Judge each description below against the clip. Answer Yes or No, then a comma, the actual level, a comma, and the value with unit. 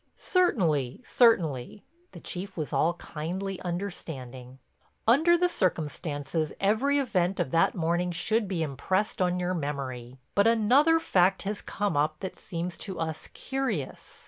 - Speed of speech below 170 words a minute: Yes, average, 140 wpm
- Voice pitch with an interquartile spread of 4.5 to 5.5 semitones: Yes, average, 5.2 semitones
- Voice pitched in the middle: Yes, medium, 180 Hz